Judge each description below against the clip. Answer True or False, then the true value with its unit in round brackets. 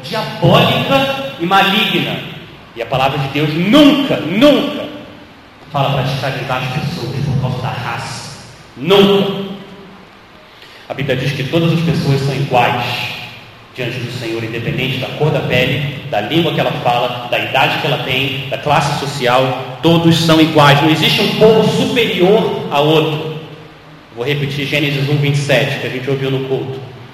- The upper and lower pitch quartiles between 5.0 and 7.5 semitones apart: False (4.3 semitones)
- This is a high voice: False (145 Hz)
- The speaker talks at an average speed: True (155 wpm)